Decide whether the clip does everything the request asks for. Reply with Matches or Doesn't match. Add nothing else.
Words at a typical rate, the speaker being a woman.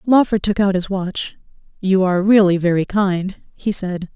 Matches